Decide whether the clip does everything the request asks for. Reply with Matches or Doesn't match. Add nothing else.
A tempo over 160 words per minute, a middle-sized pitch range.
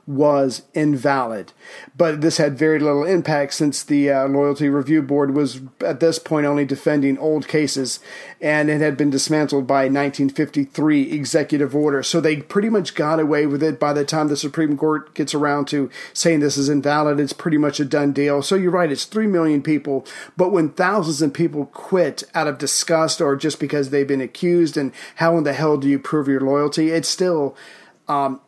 Doesn't match